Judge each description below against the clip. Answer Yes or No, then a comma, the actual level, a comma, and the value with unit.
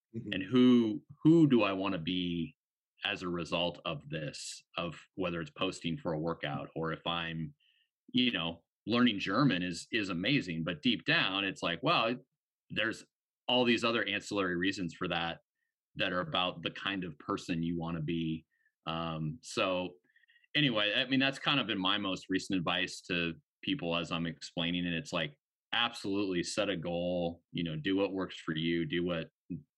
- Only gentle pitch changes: No, average, 3.6 semitones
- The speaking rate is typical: Yes, average, 180 wpm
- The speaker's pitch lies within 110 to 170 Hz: No, very low, 90 Hz